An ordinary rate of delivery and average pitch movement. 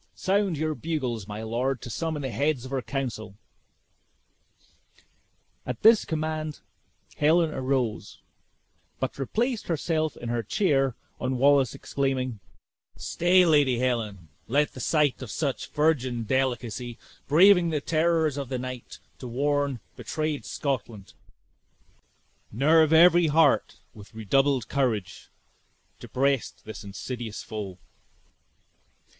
No: slow, 115 wpm; average, 4.5 semitones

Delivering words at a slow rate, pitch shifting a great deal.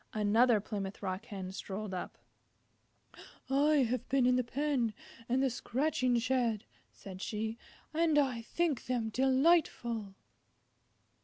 No: slow, 125 wpm; average, 4.1 semitones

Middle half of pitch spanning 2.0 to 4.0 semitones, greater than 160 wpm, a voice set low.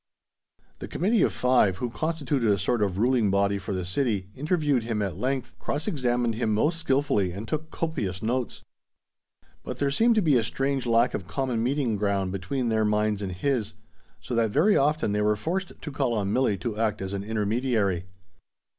No: average, 5.2 semitones; average, 190 wpm; low, 115 Hz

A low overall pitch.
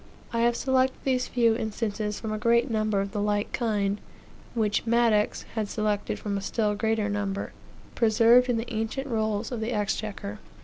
No: high, 220 Hz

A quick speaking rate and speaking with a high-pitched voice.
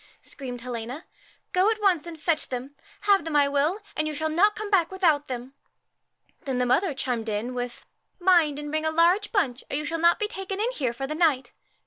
Yes: fast, 235 wpm; very high, 310 Hz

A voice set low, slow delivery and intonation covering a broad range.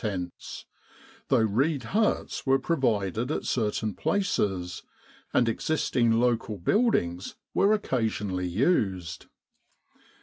Yes: low, 115 Hz; slow, 100 wpm; wide, 5.9 semitones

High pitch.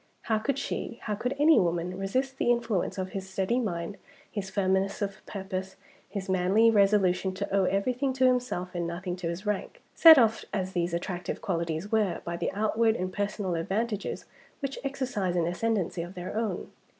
Yes: high, 195 Hz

